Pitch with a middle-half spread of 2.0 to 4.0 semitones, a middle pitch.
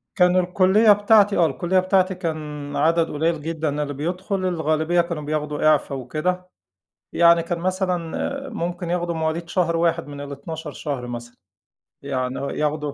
Yes: average, 3.3 semitones; medium, 165 Hz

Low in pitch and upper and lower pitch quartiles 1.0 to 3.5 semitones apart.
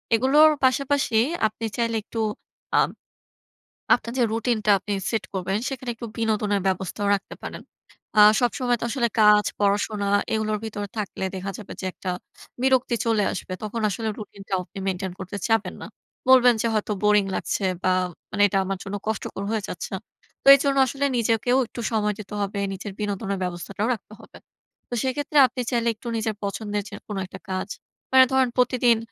No: high, 215 Hz; average, 3.2 semitones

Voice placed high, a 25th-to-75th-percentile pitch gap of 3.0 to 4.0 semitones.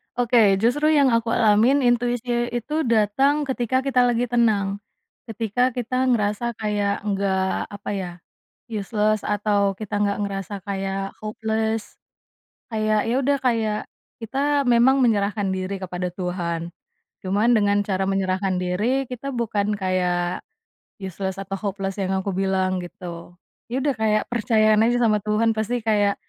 Yes: high, 215 Hz; average, 3.5 semitones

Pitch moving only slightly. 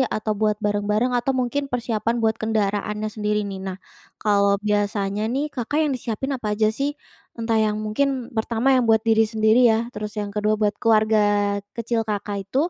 Yes: narrow, 2.0 semitones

